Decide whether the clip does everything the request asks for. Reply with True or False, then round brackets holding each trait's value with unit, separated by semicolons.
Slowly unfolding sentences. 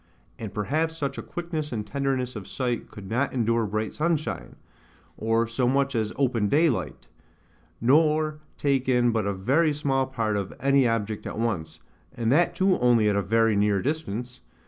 False (170 wpm)